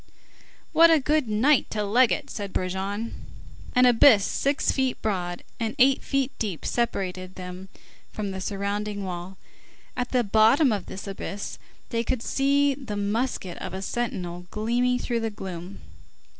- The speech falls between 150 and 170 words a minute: Yes, average, 155 wpm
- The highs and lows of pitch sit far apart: No, average, 4.6 semitones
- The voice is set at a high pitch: Yes, high, 215 Hz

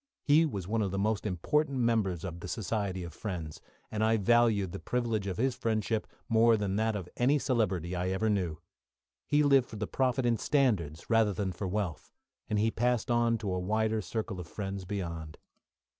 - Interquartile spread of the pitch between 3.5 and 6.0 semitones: Yes, average, 3.8 semitones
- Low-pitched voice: Yes, low, 105 Hz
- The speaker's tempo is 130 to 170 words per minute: No, average, 195 wpm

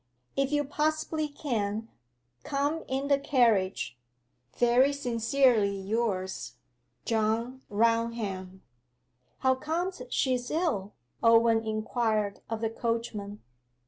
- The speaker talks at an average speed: No, slow, 95 wpm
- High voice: Yes, high, 230 Hz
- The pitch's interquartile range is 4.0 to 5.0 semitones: Yes, average, 4.3 semitones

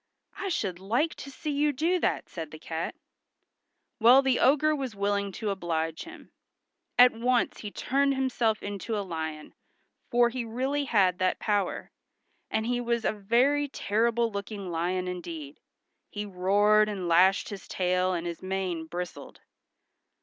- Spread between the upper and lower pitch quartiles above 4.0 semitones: Yes, average, 5.3 semitones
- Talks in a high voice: Yes, high, 205 Hz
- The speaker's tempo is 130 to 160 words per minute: Yes, average, 155 wpm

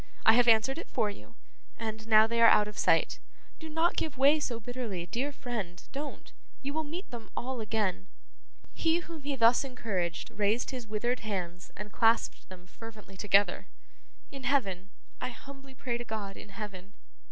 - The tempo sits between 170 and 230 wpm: Yes, average, 175 wpm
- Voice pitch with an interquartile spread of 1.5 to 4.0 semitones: No, average, 4.6 semitones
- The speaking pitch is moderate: No, high, 230 Hz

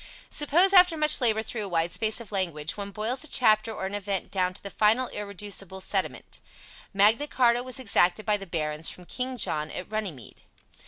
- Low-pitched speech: No, high, 210 Hz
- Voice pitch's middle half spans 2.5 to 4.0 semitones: No, average, 4.6 semitones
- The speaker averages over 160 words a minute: Yes, average, 195 wpm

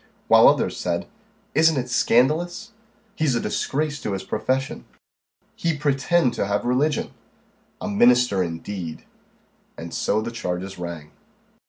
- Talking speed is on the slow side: Yes, slow, 130 wpm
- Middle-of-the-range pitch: No, low, 125 Hz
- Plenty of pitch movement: Yes, wide, 7.1 semitones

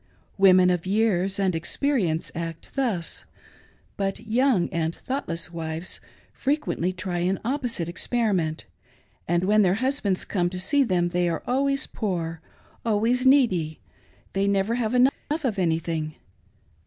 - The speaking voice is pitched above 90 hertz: Yes, high, 190 Hz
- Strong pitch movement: Yes, wide, 5.8 semitones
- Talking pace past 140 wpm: No, slow, 135 wpm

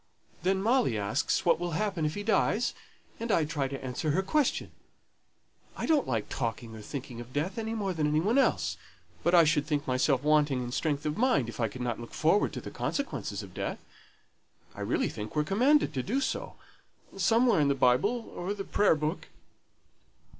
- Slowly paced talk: No, average, 195 wpm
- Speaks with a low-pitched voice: No, medium, 155 Hz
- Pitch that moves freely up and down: Yes, wide, 8.1 semitones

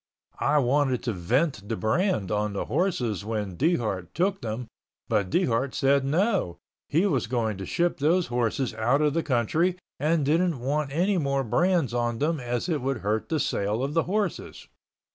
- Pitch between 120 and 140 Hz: Yes, low, 135 Hz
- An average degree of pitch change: No, wide, 6.6 semitones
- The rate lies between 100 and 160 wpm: No, average, 180 wpm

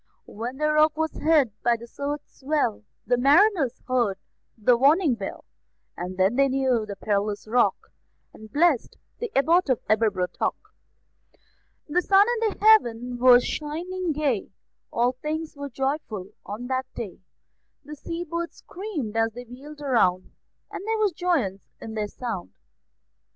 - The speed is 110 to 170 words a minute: Yes, average, 145 wpm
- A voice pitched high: Yes, very high, 260 Hz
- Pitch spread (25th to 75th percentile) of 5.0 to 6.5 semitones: Yes, wide, 5.5 semitones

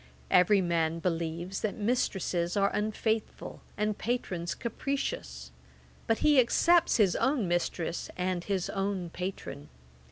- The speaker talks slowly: Yes, slow, 120 wpm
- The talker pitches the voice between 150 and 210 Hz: Yes, high, 190 Hz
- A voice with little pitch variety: No, average, 4.1 semitones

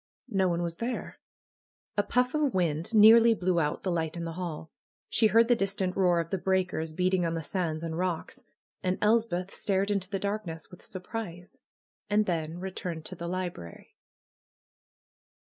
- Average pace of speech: Yes, average, 180 wpm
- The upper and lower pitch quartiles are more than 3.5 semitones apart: No, average, 3.2 semitones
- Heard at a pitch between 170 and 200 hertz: Yes, medium, 185 Hz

